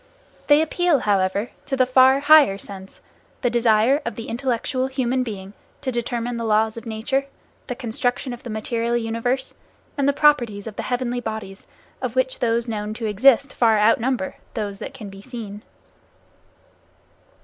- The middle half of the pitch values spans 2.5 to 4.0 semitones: Yes, average, 3.1 semitones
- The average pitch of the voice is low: No, high, 235 Hz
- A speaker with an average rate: Yes, average, 160 wpm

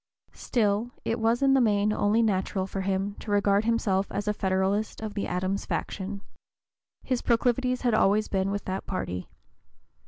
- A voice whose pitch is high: Yes, high, 205 Hz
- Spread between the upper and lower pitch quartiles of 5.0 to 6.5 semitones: No, average, 2.7 semitones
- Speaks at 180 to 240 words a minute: No, average, 165 wpm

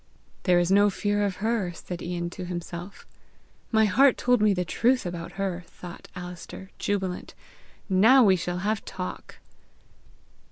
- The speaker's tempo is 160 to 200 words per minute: No, average, 150 wpm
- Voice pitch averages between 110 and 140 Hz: No, high, 190 Hz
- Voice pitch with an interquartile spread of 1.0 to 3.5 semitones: Yes, narrow, 2.6 semitones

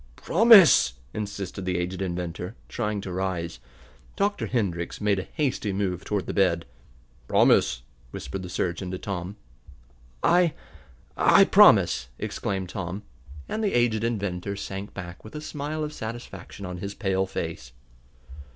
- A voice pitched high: No, very low, 95 Hz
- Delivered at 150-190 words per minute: No, average, 140 wpm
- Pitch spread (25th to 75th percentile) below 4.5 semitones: Yes, average, 3.7 semitones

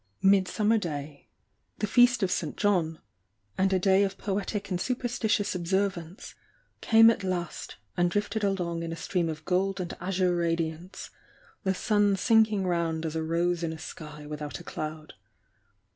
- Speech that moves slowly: No, average, 160 wpm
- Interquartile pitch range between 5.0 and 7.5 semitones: No, average, 3.4 semitones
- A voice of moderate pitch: Yes, medium, 180 Hz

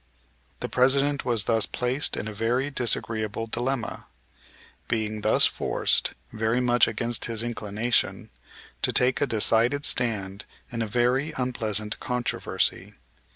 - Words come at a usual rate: No, slow, 125 wpm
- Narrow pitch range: Yes, narrow, 2.3 semitones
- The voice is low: Yes, low, 120 Hz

